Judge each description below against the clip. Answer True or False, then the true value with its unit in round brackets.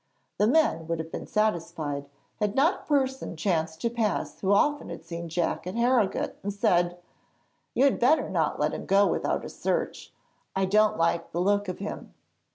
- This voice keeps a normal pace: True (185 wpm)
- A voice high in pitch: True (195 Hz)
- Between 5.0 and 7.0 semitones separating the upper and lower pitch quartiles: True (5.4 semitones)